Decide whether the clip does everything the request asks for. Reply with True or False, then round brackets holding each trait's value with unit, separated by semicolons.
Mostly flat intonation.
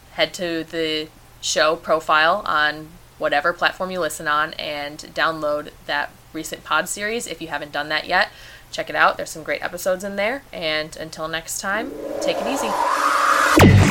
True (2.0 semitones)